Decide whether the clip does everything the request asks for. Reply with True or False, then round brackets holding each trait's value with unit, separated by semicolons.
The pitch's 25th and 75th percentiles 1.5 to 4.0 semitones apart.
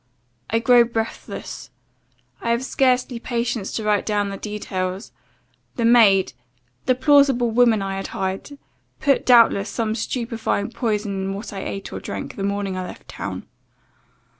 True (3.4 semitones)